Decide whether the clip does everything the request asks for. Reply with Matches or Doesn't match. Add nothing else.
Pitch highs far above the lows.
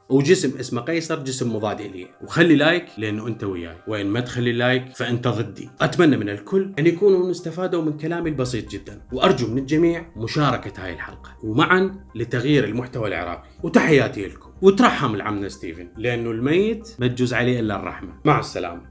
Matches